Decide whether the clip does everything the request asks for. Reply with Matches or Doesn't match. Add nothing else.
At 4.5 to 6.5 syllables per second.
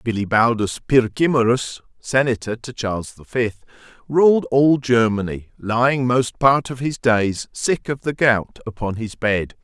Doesn't match